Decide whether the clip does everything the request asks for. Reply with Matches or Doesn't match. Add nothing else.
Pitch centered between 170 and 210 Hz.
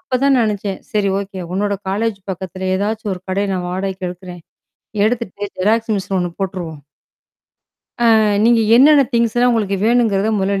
Matches